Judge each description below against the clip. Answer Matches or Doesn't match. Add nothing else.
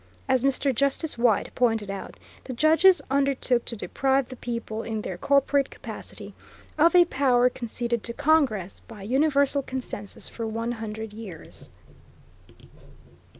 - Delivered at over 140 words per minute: Doesn't match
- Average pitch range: Matches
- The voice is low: Doesn't match